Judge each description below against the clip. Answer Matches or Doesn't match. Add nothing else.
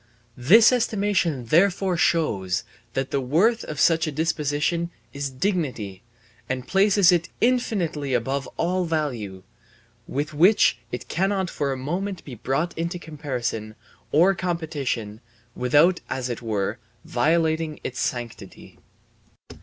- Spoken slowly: Matches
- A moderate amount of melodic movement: Doesn't match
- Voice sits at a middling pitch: Matches